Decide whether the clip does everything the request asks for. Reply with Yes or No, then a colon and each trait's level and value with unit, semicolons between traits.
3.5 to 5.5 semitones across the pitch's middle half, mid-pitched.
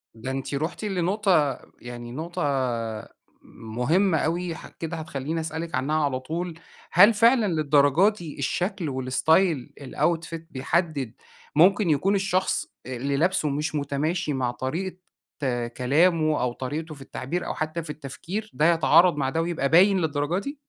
Yes: average, 4.3 semitones; medium, 160 Hz